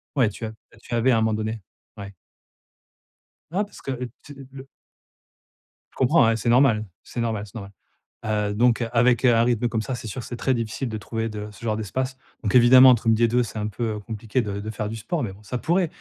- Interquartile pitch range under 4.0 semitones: Yes, average, 2.7 semitones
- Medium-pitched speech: No, low, 115 Hz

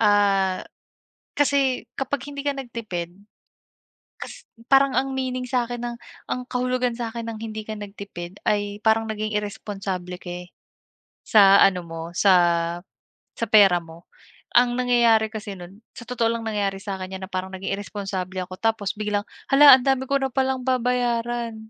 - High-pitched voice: Yes, high, 220 Hz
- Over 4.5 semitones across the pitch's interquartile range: No, average, 4.0 semitones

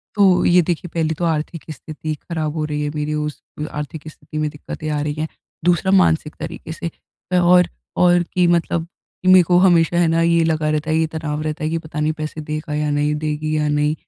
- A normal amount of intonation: No, narrow, 1.9 semitones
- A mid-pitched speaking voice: Yes, medium, 155 Hz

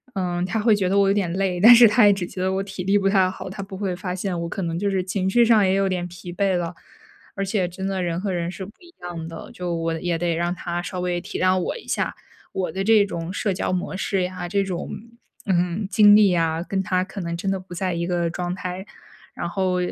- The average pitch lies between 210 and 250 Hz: No, medium, 185 Hz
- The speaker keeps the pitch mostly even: Yes, narrow, 1.9 semitones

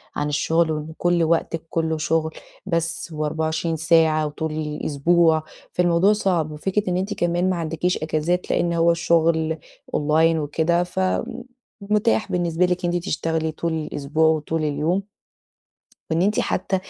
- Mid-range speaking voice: Yes, medium, 165 Hz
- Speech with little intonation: Yes, narrow, 2.0 semitones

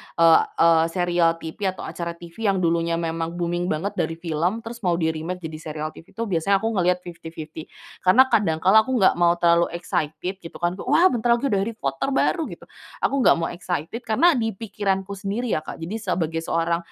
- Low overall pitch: No, medium, 175 Hz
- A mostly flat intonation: No, average, 3.4 semitones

